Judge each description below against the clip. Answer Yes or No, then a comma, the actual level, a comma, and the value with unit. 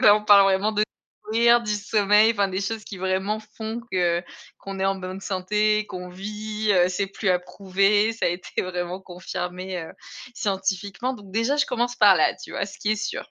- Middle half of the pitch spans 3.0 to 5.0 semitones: No, narrow, 2.4 semitones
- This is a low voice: No, high, 200 Hz